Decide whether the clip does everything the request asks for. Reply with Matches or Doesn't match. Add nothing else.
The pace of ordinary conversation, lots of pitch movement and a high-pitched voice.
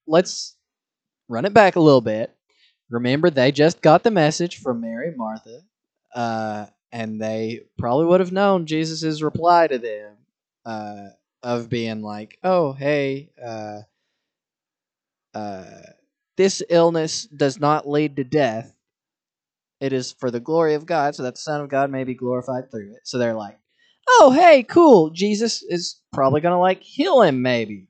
Doesn't match